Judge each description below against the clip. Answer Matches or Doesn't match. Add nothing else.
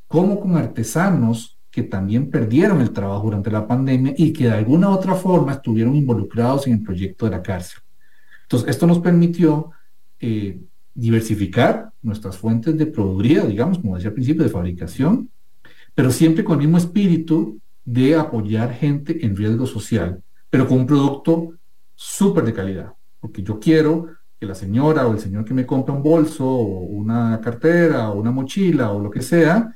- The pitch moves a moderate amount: Doesn't match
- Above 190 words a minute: Doesn't match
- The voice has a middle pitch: Doesn't match